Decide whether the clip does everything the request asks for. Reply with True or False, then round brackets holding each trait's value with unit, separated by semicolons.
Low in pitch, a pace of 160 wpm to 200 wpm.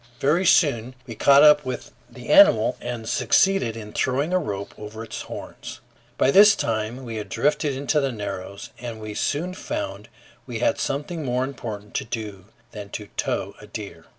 True (125 Hz; 180 wpm)